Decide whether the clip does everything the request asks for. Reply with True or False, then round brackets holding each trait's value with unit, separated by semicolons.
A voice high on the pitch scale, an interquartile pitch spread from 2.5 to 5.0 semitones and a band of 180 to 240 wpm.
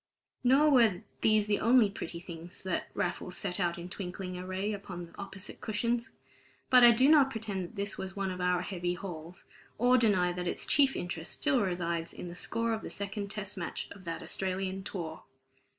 True (195 Hz; 3.8 semitones; 195 wpm)